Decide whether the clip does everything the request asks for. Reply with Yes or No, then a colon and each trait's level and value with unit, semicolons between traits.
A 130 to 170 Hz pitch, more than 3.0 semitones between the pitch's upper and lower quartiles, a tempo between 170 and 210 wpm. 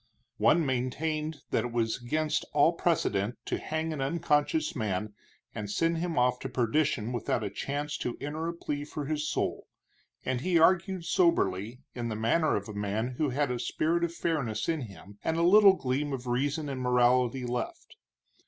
Yes: medium, 140 Hz; average, 4.8 semitones; average, 180 wpm